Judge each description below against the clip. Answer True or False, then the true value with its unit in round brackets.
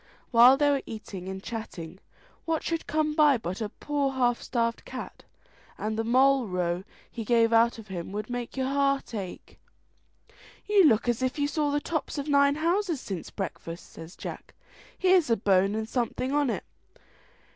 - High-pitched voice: True (240 Hz)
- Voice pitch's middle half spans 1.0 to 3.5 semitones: False (5.3 semitones)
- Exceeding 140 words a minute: True (180 wpm)